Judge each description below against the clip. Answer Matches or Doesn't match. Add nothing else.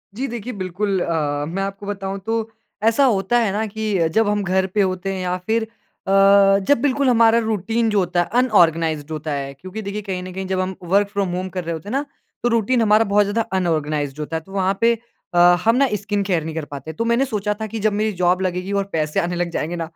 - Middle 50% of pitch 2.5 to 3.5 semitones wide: Doesn't match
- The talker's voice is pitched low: Doesn't match